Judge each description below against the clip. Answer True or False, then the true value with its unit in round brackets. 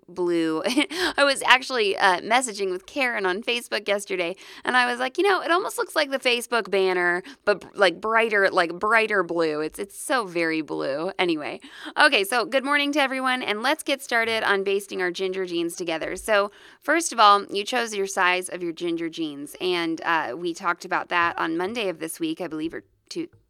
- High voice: True (205 Hz)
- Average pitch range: False (7.3 semitones)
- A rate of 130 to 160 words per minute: False (205 wpm)